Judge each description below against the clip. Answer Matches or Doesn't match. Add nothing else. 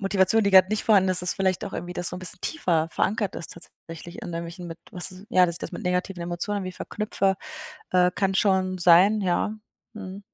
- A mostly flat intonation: Matches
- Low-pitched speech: Doesn't match